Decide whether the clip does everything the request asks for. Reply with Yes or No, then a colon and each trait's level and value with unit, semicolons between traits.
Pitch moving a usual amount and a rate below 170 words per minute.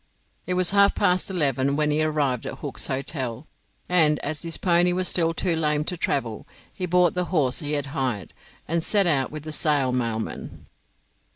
No: average, 4.4 semitones; average, 185 wpm